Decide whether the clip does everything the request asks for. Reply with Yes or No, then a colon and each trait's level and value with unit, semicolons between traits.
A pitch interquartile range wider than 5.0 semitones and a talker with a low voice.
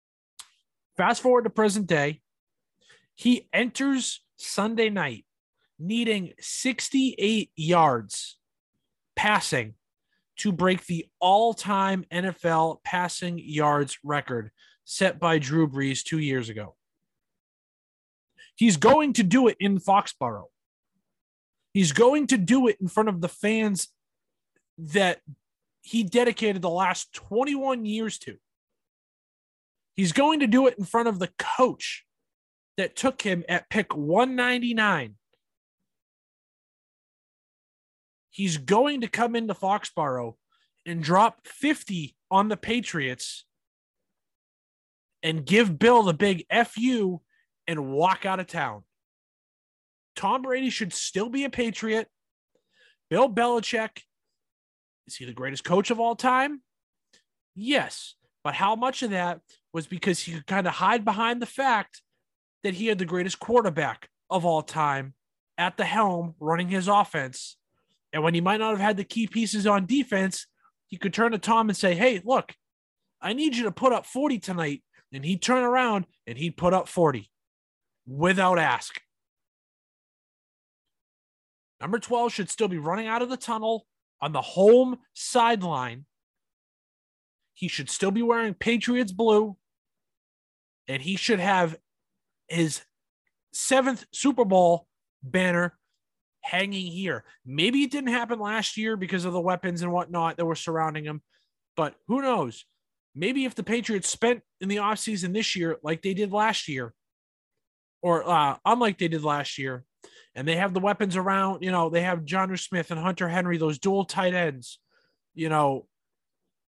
No: wide, 5.5 semitones; high, 195 Hz